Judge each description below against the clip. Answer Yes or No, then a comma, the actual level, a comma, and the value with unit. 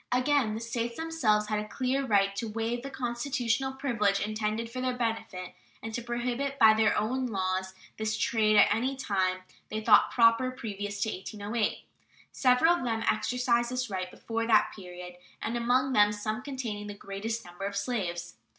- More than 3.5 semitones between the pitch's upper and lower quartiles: No, average, 3.2 semitones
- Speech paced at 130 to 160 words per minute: No, average, 175 wpm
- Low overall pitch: No, high, 225 Hz